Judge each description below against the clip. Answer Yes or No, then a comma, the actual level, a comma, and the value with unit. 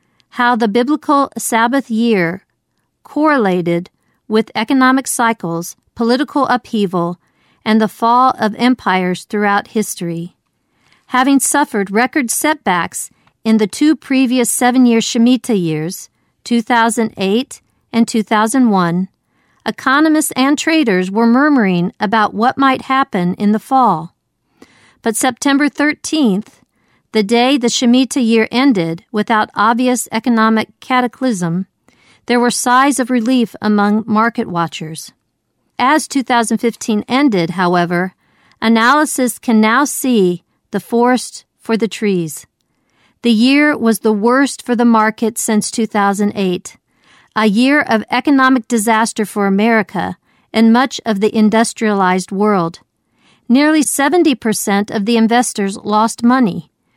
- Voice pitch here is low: No, high, 225 Hz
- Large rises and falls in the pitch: No, average, 3.7 semitones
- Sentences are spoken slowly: Yes, slow, 115 wpm